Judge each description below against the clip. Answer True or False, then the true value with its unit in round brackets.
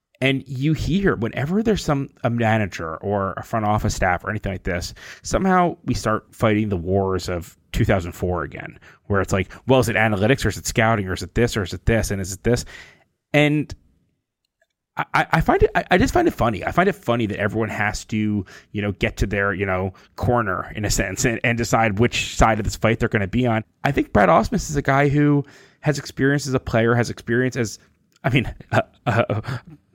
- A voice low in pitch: True (115 Hz)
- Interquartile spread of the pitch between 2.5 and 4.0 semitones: False (4.8 semitones)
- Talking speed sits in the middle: False (220 wpm)